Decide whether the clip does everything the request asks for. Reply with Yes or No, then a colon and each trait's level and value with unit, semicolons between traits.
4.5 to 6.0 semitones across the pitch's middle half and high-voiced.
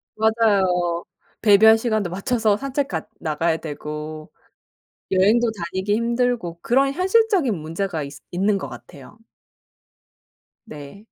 Yes: wide, 5.5 semitones; high, 200 Hz